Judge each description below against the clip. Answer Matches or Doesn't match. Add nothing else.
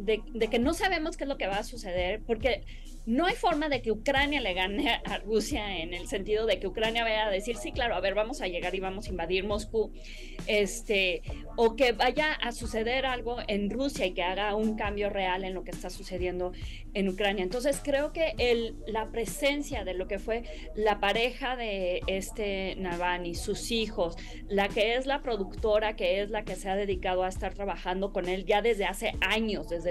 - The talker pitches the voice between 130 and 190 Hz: Doesn't match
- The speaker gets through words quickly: Matches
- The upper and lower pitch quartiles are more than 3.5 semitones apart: Matches